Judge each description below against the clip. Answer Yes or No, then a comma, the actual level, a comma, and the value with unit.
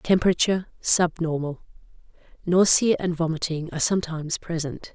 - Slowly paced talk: Yes, slow, 95 wpm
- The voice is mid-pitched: Yes, medium, 170 Hz